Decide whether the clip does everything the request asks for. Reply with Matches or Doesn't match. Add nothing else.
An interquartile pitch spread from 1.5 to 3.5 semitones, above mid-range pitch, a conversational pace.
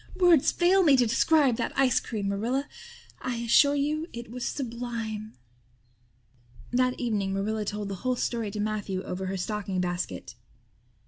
Doesn't match